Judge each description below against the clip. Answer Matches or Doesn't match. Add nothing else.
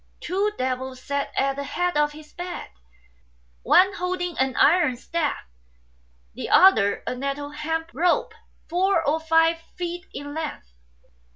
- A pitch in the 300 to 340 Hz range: Matches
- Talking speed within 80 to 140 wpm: Matches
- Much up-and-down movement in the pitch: Doesn't match